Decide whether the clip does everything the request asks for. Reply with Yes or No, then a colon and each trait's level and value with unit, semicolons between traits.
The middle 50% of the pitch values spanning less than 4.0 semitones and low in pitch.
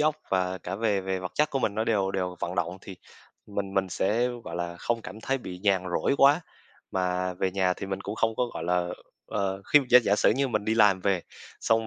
Yes: average, 3.4 semitones; very low, 95 Hz